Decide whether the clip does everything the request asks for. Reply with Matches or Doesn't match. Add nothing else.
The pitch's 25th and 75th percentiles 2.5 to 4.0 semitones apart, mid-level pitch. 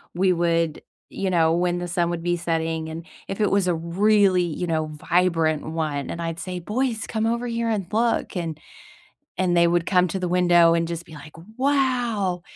Matches